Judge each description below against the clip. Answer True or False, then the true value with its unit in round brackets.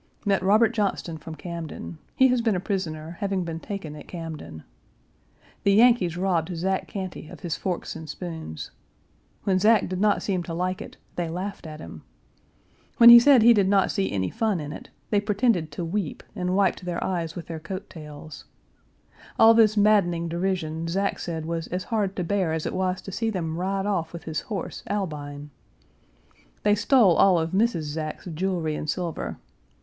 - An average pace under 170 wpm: False (185 wpm)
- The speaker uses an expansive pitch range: False (3.7 semitones)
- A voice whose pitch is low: False (180 Hz)